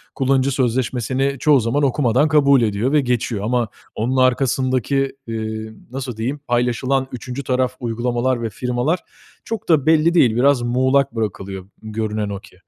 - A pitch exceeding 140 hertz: No, low, 125 Hz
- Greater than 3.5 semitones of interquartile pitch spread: No, average, 3.1 semitones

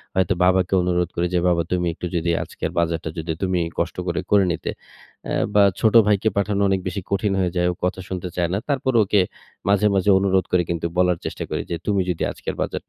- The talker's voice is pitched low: Yes, very low, 90 Hz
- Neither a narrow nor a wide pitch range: No, narrow, 2.1 semitones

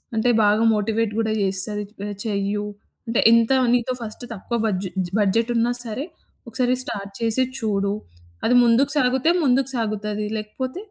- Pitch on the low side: No, high, 225 Hz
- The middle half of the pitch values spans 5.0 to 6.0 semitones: No, average, 2.8 semitones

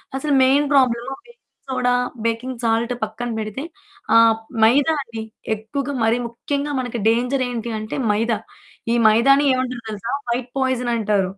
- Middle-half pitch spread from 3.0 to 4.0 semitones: No, narrow, 2.6 semitones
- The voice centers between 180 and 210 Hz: No, high, 240 Hz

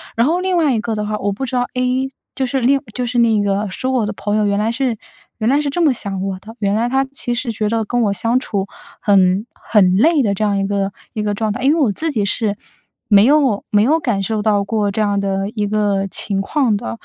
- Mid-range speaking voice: No, high, 215 Hz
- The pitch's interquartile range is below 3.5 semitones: No, average, 3.9 semitones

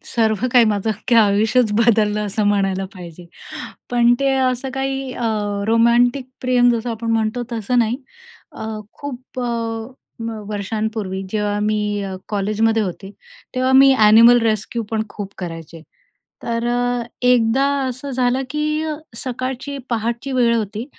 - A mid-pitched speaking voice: No, high, 230 Hz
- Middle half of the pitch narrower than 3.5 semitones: Yes, average, 2.9 semitones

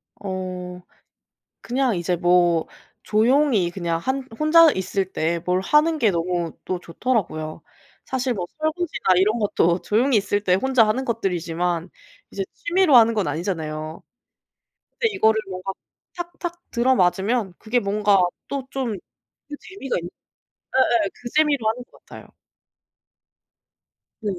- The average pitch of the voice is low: No, high, 210 Hz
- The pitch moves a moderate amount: No, wide, 6.5 semitones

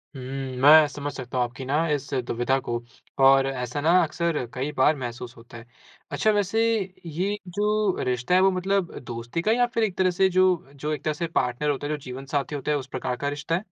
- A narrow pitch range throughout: No, wide, 5.6 semitones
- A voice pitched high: No, medium, 150 Hz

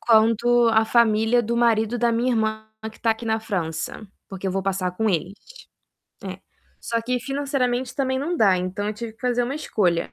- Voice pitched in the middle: No, high, 225 Hz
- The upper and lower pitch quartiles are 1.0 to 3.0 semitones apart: Yes, narrow, 2.5 semitones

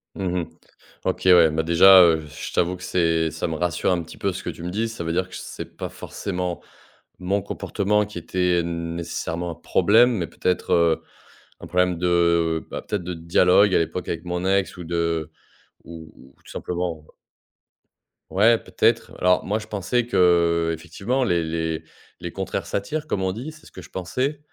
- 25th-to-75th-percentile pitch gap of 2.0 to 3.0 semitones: Yes, average, 2.7 semitones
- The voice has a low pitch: Yes, very low, 90 Hz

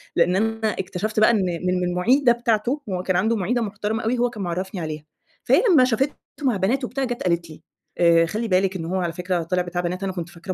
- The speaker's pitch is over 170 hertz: Yes, high, 190 Hz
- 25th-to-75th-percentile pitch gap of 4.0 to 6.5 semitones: Yes, average, 4.3 semitones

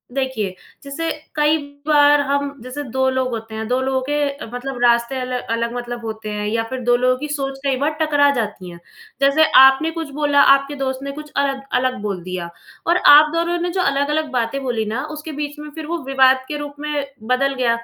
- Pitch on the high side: Yes, very high, 270 Hz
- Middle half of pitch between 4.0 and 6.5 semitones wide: No, average, 3.2 semitones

